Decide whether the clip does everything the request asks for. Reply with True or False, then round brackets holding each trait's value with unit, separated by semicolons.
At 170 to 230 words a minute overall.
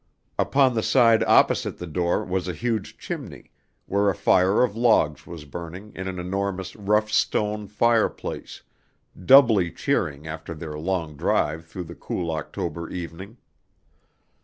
False (140 wpm)